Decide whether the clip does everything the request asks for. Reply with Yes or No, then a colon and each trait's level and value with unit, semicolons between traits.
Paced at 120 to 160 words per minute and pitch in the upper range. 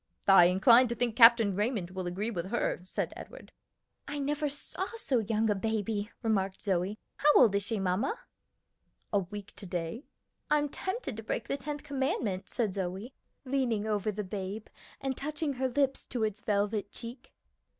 No: average, 170 wpm; high, 220 Hz